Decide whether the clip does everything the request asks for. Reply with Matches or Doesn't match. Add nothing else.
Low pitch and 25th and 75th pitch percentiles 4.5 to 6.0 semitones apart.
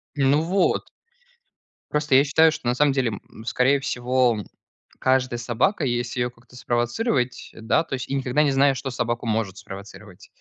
Doesn't match